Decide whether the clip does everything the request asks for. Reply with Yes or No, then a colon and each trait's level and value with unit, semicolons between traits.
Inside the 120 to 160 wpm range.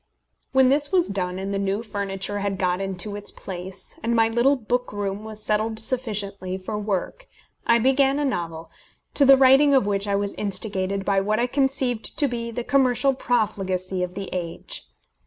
No: average, 185 wpm